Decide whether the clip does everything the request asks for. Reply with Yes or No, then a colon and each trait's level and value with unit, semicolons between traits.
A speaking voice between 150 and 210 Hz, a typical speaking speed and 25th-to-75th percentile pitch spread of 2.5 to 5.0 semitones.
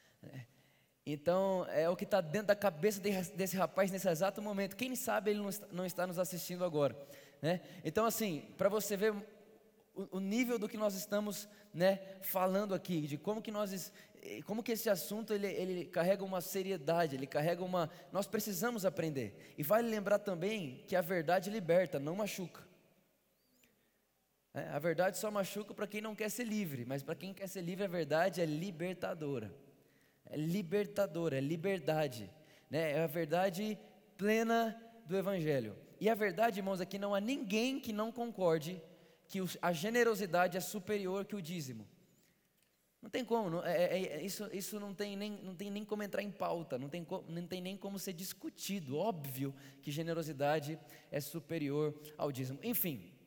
Yes: high, 190 Hz; average, 175 wpm; average, 3.9 semitones